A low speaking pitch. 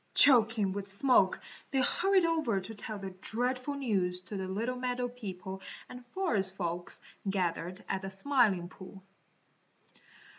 No: high, 205 Hz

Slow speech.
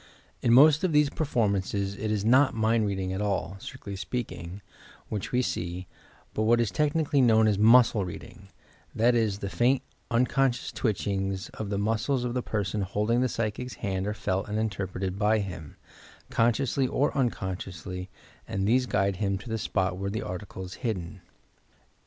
No: average, 180 wpm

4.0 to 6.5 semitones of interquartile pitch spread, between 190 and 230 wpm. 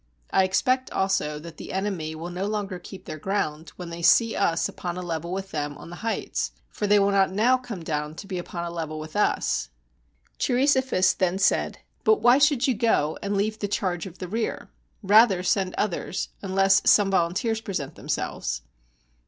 No: average, 3.6 semitones; average, 195 wpm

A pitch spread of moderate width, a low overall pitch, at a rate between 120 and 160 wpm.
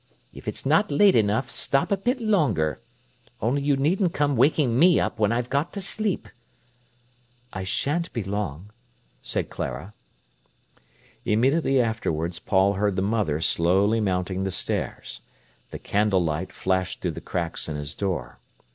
No: wide, 7.4 semitones; low, 105 Hz; average, 145 wpm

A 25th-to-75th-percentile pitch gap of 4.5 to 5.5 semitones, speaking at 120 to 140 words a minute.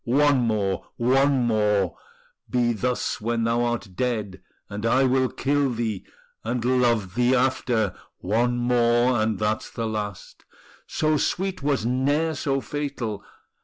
No: average, 3.2 semitones; slow, 135 wpm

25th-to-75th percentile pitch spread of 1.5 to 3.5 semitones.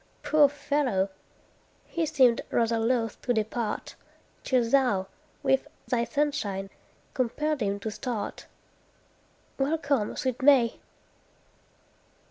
No: average, 4.2 semitones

